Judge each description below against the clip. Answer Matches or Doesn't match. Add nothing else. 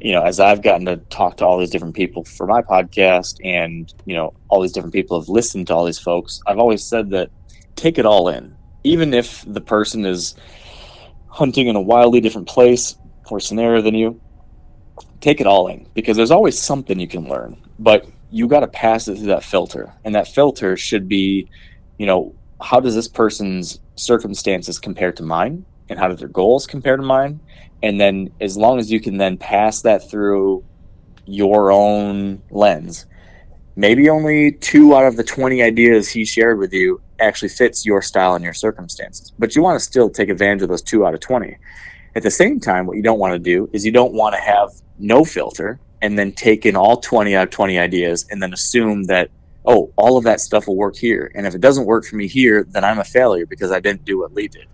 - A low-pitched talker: Matches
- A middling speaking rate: Doesn't match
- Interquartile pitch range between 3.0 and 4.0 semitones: Doesn't match